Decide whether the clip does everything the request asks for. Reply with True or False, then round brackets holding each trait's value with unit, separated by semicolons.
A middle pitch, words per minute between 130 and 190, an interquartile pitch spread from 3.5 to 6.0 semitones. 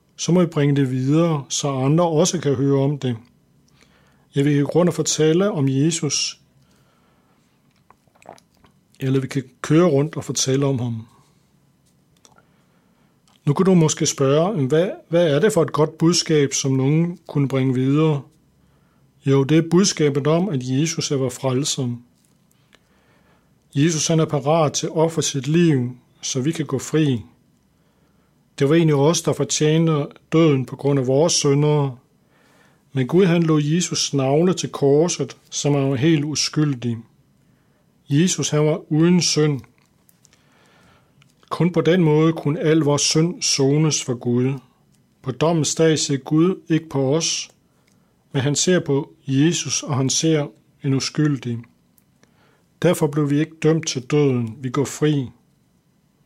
False (150 Hz; 150 wpm; 2.7 semitones)